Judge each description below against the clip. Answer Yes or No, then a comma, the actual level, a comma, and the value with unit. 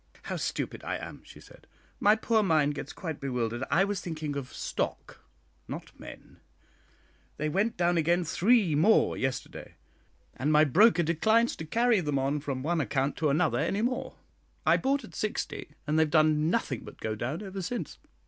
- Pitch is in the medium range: Yes, medium, 160 Hz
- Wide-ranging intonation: Yes, wide, 6.0 semitones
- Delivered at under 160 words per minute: No, average, 185 wpm